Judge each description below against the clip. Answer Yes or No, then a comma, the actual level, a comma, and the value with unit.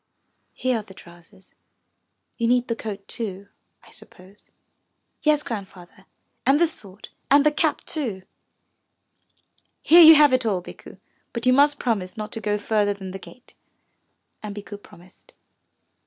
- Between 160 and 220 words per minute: No, average, 150 wpm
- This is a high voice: Yes, high, 215 Hz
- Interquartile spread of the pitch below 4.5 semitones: No, average, 4.9 semitones